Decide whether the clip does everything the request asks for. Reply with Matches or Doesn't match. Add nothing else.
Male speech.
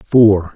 Matches